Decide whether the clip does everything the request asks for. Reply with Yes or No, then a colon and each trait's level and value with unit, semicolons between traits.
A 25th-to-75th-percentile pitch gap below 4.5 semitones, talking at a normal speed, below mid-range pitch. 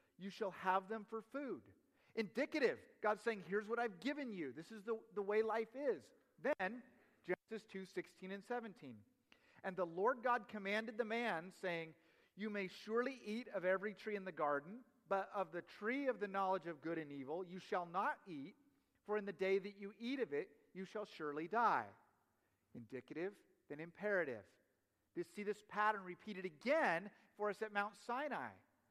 No: average, 4.0 semitones; average, 180 wpm; high, 205 Hz